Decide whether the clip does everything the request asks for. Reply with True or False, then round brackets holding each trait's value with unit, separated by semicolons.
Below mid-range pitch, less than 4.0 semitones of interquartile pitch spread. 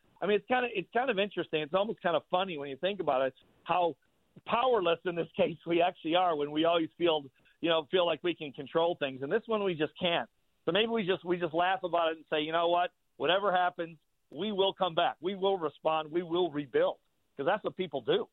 False (175 Hz; 2.7 semitones)